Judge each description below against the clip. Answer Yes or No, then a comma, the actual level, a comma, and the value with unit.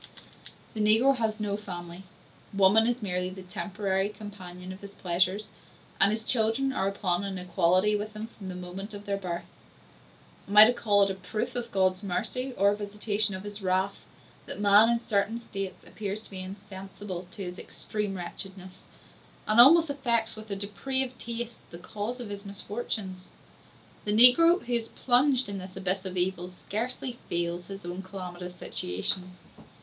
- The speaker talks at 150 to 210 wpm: Yes, average, 175 wpm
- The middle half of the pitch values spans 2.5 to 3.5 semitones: Yes, average, 2.9 semitones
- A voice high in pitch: Yes, high, 200 Hz